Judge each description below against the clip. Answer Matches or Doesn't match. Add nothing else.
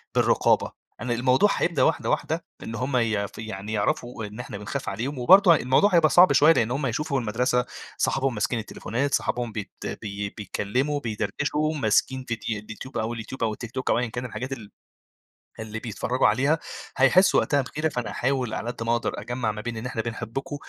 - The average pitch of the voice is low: Matches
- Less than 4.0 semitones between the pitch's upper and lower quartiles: Matches